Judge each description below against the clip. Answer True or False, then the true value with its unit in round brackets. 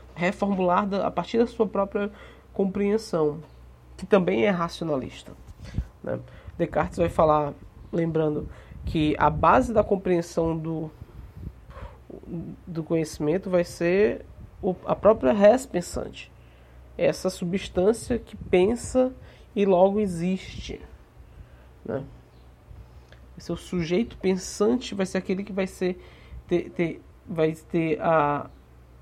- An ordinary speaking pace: False (110 wpm)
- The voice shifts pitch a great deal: False (4.5 semitones)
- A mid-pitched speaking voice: True (175 Hz)